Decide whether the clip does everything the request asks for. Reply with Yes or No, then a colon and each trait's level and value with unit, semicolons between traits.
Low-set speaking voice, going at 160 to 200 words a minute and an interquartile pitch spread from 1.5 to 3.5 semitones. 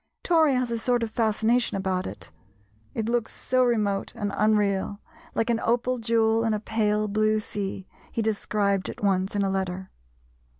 No: high, 215 Hz; average, 170 wpm; narrow, 2.5 semitones